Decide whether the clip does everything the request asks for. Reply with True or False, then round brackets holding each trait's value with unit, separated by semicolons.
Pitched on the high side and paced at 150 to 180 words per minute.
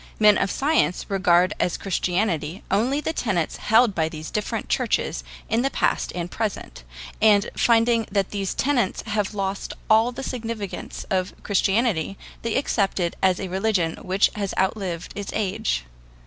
True (200 Hz; 155 wpm)